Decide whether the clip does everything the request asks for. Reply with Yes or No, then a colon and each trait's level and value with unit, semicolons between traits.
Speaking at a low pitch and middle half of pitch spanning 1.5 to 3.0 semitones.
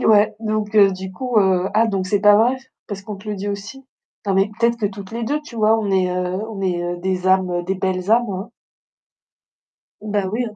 No: high, 200 Hz; narrow, 2.5 semitones